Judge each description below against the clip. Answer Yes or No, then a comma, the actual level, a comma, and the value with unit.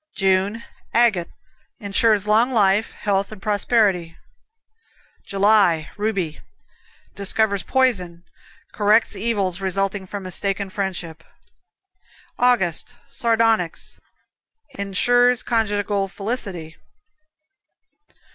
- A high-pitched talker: Yes, high, 200 Hz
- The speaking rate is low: Yes, slow, 75 wpm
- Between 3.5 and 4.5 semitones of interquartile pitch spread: No, average, 2.8 semitones